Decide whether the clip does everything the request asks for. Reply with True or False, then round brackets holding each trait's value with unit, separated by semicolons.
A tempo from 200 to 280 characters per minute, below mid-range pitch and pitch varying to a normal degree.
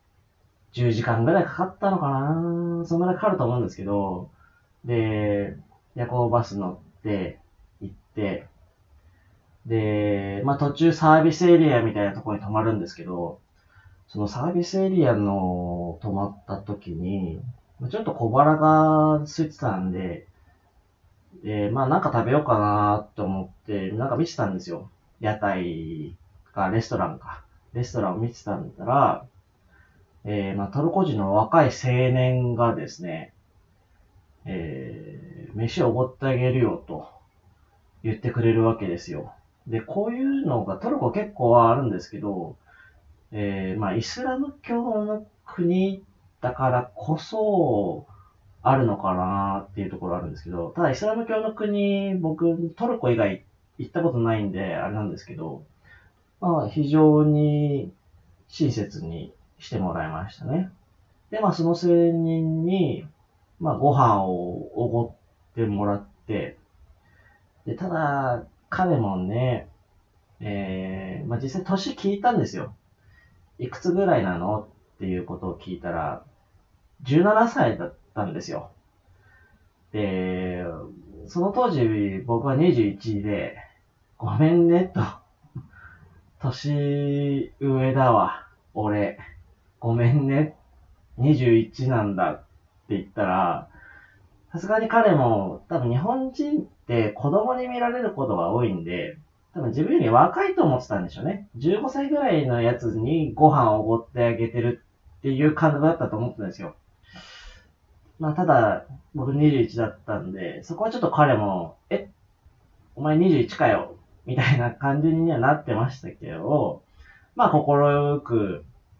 False (260 characters per minute; 115 Hz; 8.0 semitones)